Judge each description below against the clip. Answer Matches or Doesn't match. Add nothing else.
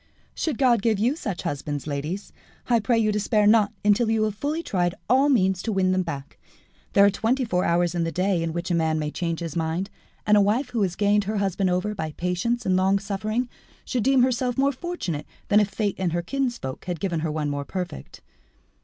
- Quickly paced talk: Matches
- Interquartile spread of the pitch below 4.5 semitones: Doesn't match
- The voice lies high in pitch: Matches